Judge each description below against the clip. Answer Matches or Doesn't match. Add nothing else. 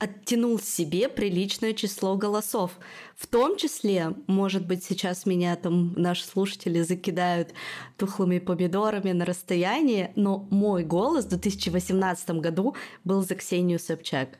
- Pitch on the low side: Doesn't match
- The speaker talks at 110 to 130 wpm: Matches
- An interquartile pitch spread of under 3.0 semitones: Matches